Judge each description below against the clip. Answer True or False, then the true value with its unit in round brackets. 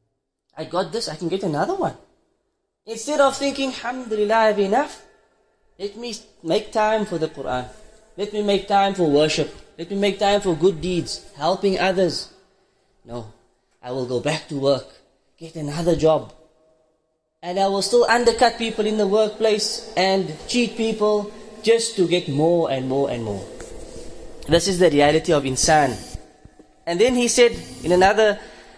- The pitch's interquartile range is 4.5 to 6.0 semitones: True (5.6 semitones)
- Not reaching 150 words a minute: False (165 wpm)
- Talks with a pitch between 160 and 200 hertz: True (190 Hz)